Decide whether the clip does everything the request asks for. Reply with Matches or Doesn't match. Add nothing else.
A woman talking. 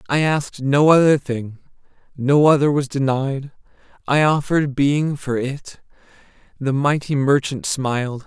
Doesn't match